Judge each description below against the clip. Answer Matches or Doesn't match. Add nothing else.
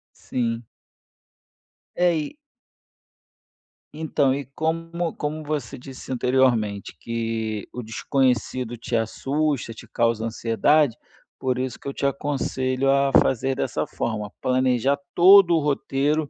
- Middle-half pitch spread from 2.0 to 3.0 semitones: Doesn't match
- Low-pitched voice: Matches